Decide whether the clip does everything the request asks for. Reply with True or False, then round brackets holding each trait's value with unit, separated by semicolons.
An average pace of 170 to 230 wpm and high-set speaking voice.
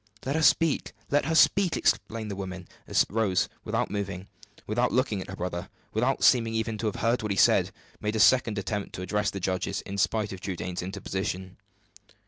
False (195 wpm; 105 Hz)